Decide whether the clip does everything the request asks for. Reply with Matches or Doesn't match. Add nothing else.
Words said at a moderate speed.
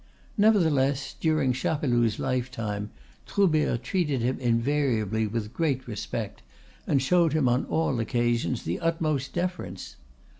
Doesn't match